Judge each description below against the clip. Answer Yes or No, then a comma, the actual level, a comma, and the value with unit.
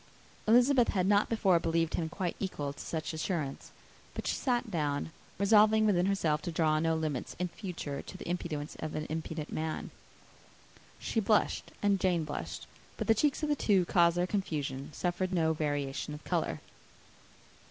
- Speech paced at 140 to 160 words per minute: No, average, 175 wpm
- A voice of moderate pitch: Yes, medium, 170 Hz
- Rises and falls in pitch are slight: No, average, 4.3 semitones